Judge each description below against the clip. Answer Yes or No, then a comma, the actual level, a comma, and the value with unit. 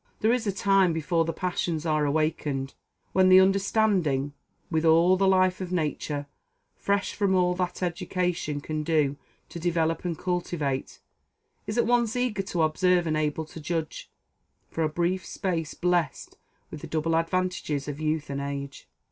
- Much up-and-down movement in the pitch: No, average, 3.2 semitones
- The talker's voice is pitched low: No, medium, 170 Hz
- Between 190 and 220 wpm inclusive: No, average, 165 wpm